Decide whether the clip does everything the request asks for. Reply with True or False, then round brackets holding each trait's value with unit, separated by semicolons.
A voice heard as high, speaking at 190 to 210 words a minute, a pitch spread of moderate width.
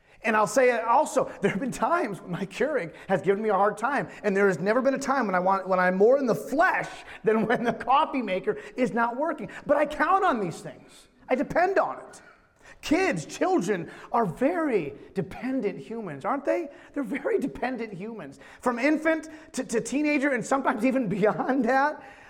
True (255 Hz; 200 wpm; 4.9 semitones)